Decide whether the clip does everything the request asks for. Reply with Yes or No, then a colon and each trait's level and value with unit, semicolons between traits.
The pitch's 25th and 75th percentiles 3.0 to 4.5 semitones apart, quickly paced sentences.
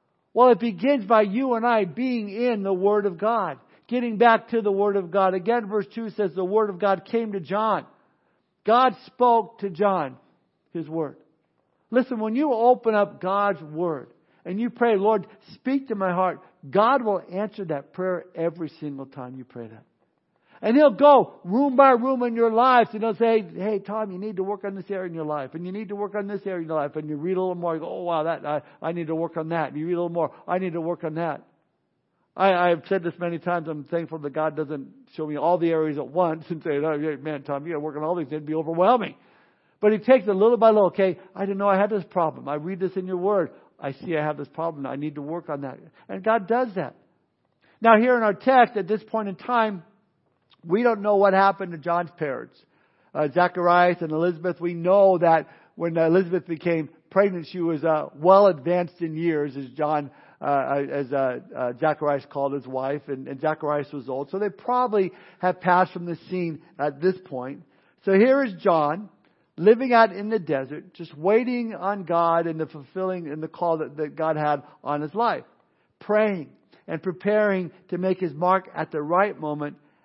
No: average, 4.9 semitones; fast, 225 wpm